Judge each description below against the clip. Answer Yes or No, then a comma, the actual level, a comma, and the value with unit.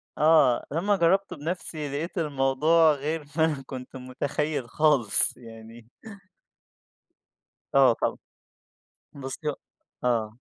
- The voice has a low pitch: No, medium, 145 Hz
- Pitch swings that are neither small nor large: Yes, average, 4.0 semitones